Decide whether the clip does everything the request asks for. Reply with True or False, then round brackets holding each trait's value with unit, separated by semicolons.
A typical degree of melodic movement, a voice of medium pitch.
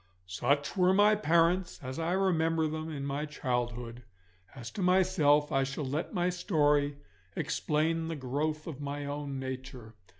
True (3.3 semitones; 150 Hz)